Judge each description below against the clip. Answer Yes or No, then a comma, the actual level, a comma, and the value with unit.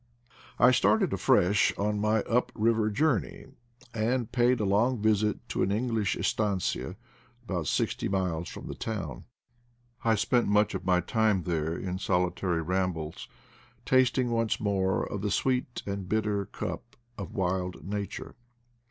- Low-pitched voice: Yes, low, 105 Hz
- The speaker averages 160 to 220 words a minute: No, average, 145 wpm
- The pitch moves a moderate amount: Yes, average, 3.6 semitones